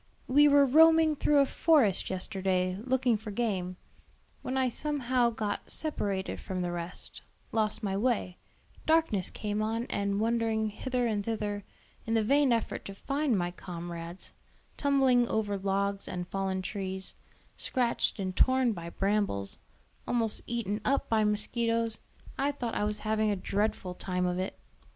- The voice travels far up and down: No, average, 4.4 semitones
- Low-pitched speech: No, high, 215 Hz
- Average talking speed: Yes, average, 150 wpm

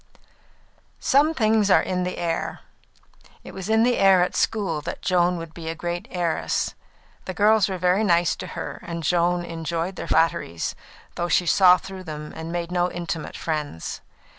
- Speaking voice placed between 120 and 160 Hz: No, medium, 175 Hz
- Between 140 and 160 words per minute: No, average, 175 wpm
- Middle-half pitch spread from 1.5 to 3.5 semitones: Yes, narrow, 2.4 semitones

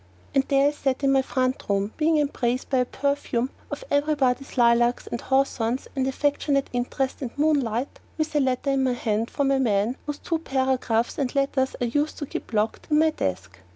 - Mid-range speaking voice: No, very high, 265 Hz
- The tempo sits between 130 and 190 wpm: No, average, 200 wpm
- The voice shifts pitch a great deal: No, average, 3.0 semitones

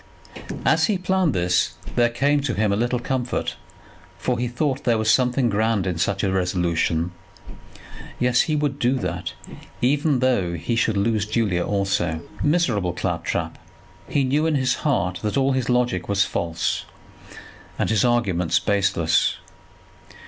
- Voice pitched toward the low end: Yes, low, 115 Hz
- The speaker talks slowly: No, average, 155 wpm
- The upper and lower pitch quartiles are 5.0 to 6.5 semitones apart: Yes, wide, 5.6 semitones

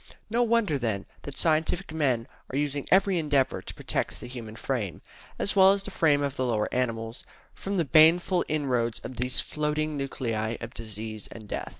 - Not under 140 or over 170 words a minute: No, average, 185 wpm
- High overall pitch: No, medium, 140 Hz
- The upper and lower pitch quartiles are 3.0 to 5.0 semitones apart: No, wide, 5.6 semitones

